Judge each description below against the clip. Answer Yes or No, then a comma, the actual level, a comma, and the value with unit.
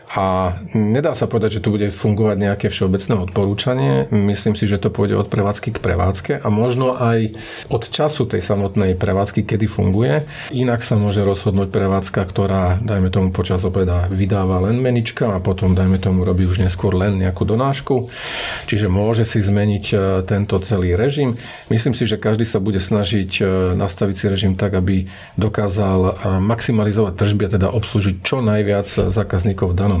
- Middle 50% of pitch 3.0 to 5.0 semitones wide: No, narrow, 2.5 semitones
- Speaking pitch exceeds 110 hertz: No, low, 105 Hz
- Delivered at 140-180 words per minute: Yes, fast, 165 wpm